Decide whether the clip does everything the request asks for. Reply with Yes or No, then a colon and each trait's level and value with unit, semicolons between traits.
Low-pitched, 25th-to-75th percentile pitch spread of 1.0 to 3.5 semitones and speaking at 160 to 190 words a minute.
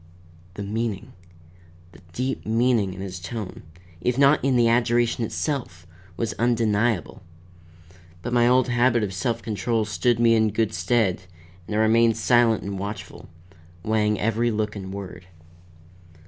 No: low, 115 Hz; average, 2.8 semitones; average, 145 wpm